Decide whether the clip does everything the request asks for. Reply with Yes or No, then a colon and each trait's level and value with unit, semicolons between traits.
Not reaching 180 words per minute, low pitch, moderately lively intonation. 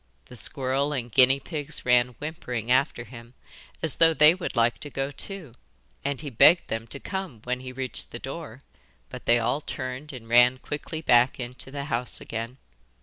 No: average, 185 wpm; low, 130 Hz; average, 3.3 semitones